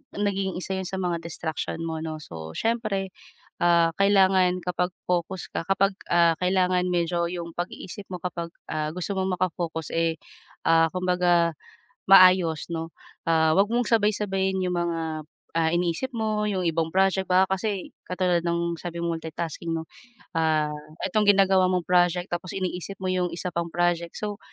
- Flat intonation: Yes, narrow, 2.3 semitones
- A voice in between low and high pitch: Yes, medium, 180 Hz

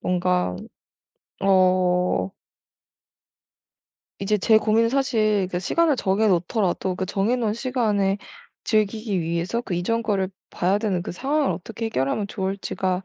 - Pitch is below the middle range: No, high, 195 Hz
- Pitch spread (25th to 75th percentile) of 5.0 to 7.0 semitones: No, average, 3.5 semitones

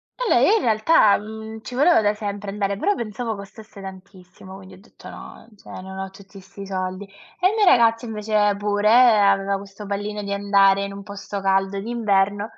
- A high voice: Yes, high, 200 Hz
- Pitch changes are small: Yes, narrow, 1.9 semitones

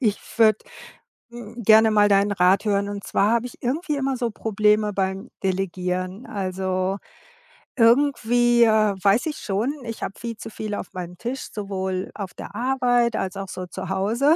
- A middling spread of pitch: Yes, average, 3.7 semitones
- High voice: Yes, high, 210 Hz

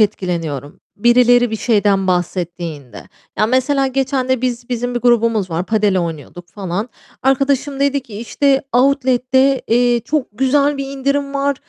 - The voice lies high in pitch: Yes, high, 245 Hz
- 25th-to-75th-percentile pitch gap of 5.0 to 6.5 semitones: Yes, wide, 5.4 semitones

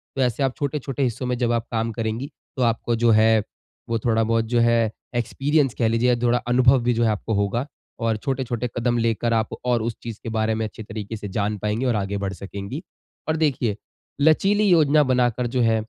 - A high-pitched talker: No, low, 115 Hz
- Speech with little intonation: Yes, narrow, 2.2 semitones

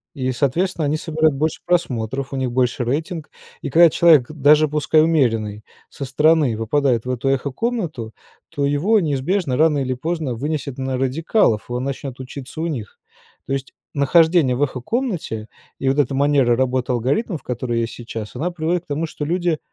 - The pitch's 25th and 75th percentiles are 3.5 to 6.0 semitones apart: Yes, average, 4.0 semitones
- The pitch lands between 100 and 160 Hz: Yes, medium, 140 Hz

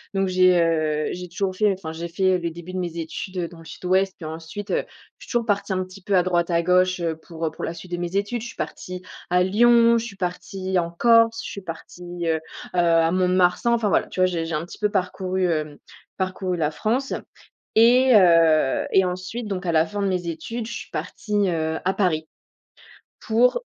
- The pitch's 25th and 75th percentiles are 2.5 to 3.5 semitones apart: Yes, average, 2.9 semitones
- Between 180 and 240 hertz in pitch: Yes, medium, 185 Hz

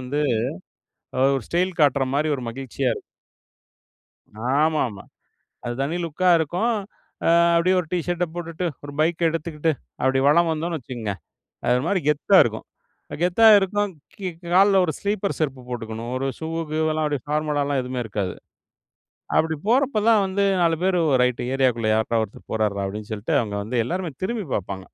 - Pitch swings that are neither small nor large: No, wide, 6.2 semitones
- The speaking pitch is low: No, medium, 150 Hz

